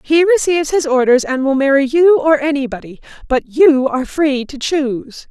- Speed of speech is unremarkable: Yes, average, 180 wpm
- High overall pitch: Yes, very high, 285 Hz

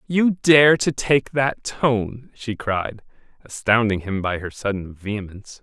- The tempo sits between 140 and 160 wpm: Yes, average, 150 wpm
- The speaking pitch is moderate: No, low, 115 Hz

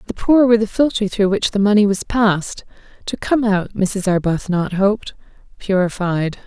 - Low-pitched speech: No, high, 200 Hz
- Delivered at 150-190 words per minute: Yes, average, 165 wpm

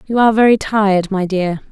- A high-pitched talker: Yes, high, 205 Hz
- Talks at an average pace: No, fast, 210 wpm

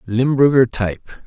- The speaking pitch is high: No, low, 120 Hz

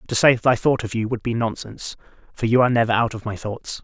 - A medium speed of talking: No, fast, 280 wpm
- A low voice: Yes, low, 115 Hz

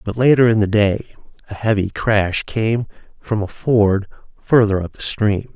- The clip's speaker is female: No, male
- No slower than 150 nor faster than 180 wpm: Yes, average, 175 wpm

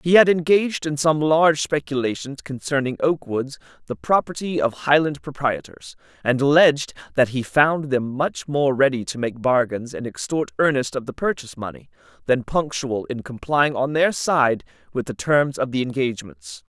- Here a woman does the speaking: No, male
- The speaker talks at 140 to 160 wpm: No, average, 170 wpm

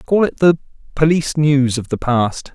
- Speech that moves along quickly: No, average, 190 wpm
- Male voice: Yes, male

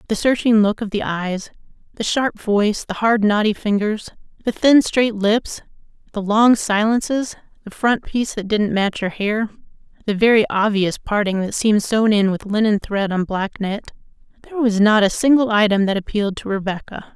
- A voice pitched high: Yes, high, 210 Hz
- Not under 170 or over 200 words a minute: Yes, average, 180 wpm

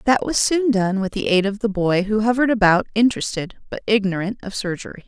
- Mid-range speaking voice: No, high, 210 Hz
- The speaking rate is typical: No, fast, 215 wpm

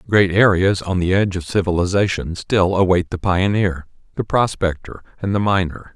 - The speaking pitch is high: No, very low, 95 Hz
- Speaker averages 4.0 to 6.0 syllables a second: Yes, 5.1 syllables/s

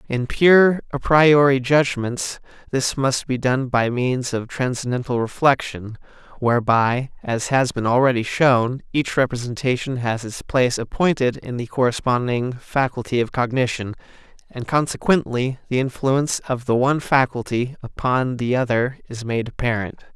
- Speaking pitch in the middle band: No, low, 125 Hz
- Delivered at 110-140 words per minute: Yes, slow, 135 wpm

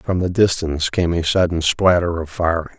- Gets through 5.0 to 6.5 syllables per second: Yes, 5.3 syllables/s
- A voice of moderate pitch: No, very low, 85 Hz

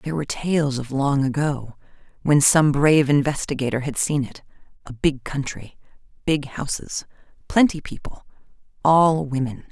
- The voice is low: No, medium, 145 Hz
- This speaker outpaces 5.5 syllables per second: No, 5.0 syllables/s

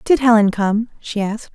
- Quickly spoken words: No, average, 195 wpm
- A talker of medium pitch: No, high, 220 Hz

